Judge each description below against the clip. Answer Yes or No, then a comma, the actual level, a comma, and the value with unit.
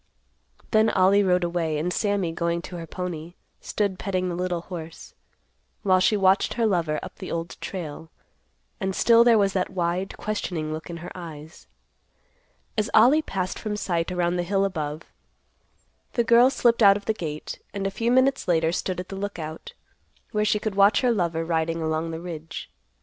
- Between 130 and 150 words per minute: No, average, 180 wpm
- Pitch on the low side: No, medium, 180 Hz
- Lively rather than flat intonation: No, average, 3.5 semitones